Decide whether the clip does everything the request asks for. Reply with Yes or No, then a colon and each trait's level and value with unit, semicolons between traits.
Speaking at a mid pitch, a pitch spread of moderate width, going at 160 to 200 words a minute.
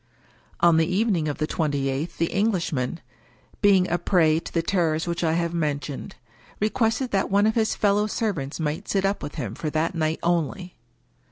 Yes: medium, 170 Hz; average, 4.2 semitones; average, 190 wpm